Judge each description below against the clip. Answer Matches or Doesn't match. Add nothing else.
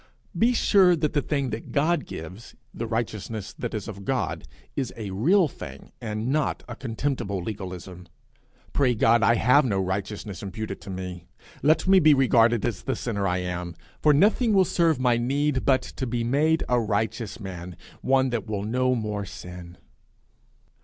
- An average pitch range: Doesn't match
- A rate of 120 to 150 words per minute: Doesn't match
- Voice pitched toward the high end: Doesn't match